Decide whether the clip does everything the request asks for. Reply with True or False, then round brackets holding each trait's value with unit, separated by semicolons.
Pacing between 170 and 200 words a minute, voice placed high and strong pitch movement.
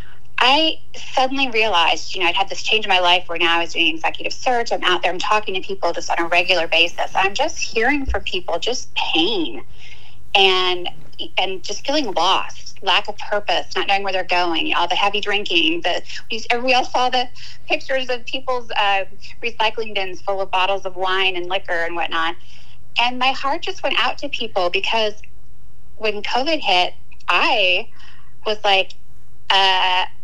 True (180 wpm; 210 Hz; 6.3 semitones)